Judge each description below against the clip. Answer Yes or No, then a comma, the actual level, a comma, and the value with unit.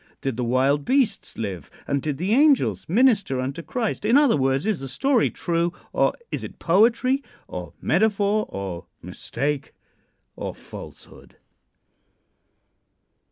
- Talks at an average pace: No, slow, 130 wpm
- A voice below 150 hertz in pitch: No, medium, 170 Hz